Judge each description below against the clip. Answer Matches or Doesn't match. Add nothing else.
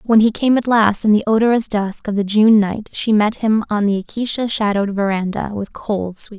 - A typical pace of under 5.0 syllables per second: Doesn't match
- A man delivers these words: Doesn't match